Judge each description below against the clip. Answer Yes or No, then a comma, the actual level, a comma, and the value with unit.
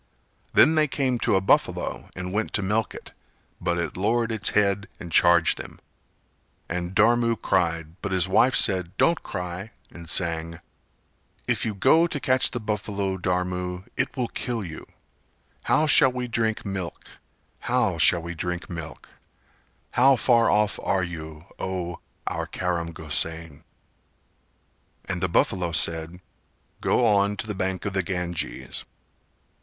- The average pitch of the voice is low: Yes, very low, 95 Hz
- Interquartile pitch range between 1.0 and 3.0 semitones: No, average, 4.2 semitones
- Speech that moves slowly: No, average, 150 wpm